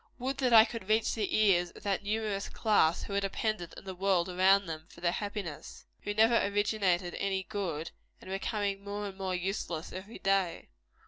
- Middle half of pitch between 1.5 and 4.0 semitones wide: Yes, narrow, 2.6 semitones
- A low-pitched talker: No, high, 195 Hz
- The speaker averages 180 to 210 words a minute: Yes, average, 190 wpm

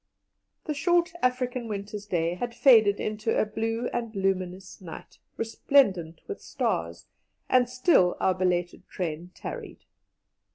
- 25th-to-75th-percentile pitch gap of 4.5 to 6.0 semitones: Yes, average, 5.2 semitones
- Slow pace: Yes, slow, 125 wpm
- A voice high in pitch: Yes, high, 210 Hz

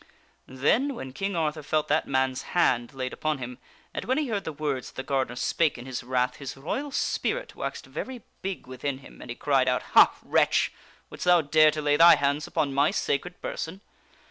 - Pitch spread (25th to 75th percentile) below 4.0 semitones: No, average, 4.5 semitones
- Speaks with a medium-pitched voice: Yes, medium, 145 Hz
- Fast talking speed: Yes, fast, 210 wpm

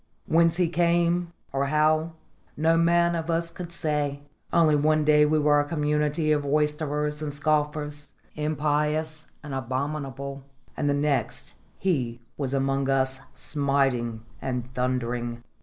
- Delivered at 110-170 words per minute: Yes, slow, 135 wpm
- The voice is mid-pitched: Yes, medium, 150 Hz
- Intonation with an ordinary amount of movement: No, narrow, 2.2 semitones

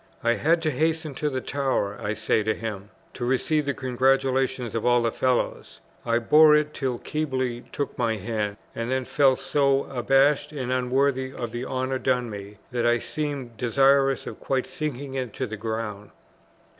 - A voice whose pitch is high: No, low, 130 Hz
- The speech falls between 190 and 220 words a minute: No, average, 175 wpm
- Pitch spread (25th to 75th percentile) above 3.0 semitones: No, average, 2.7 semitones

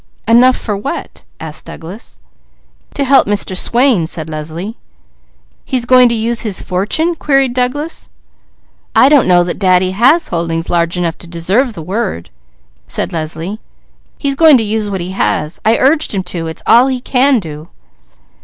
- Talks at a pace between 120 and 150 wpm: No, average, 165 wpm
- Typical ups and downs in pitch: No, wide, 6.8 semitones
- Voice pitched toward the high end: Yes, high, 205 Hz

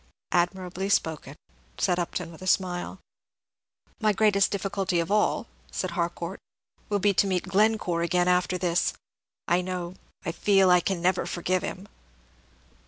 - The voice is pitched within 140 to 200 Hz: Yes, medium, 185 Hz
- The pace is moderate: Yes, average, 145 wpm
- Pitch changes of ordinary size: No, narrow, 1.9 semitones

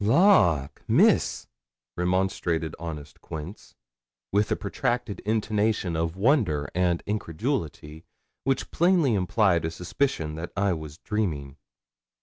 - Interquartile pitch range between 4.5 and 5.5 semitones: Yes, average, 5.2 semitones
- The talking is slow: Yes, slow, 110 wpm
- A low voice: Yes, very low, 90 Hz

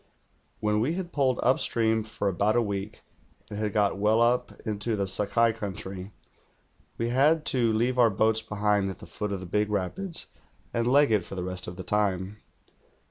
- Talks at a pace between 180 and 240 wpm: Yes, average, 190 wpm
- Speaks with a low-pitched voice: Yes, low, 105 Hz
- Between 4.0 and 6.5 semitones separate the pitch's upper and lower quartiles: No, average, 2.9 semitones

